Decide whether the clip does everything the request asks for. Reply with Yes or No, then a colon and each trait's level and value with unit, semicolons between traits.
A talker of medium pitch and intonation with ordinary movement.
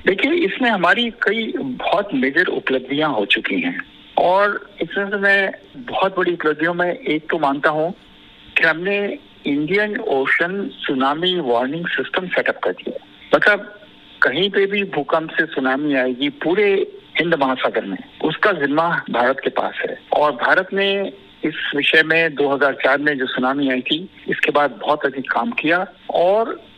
No: medium, 175 Hz; wide, 6.0 semitones